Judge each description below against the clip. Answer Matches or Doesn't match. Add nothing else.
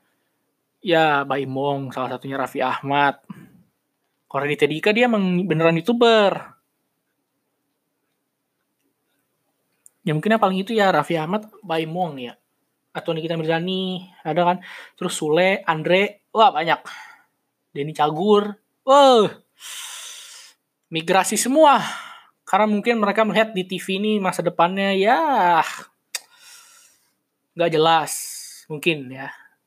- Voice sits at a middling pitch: Matches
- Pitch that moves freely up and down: Matches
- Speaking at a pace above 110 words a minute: Doesn't match